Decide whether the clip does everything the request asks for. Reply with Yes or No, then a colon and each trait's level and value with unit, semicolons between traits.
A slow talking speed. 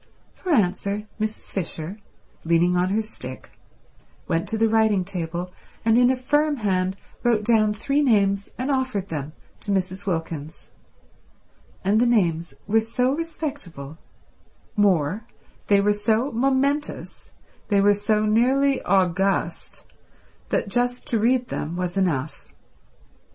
Yes: slow, 130 wpm